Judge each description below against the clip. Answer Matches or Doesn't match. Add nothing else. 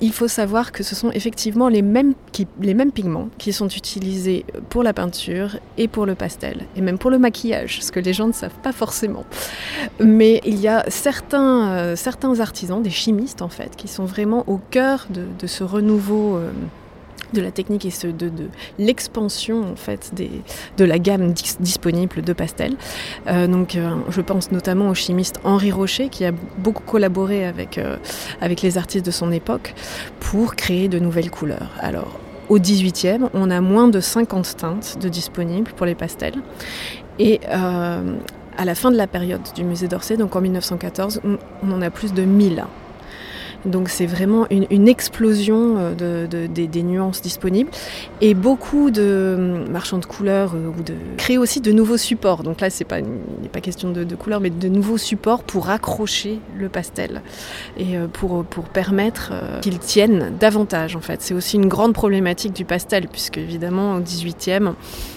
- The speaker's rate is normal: Matches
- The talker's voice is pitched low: Doesn't match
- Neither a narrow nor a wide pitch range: Matches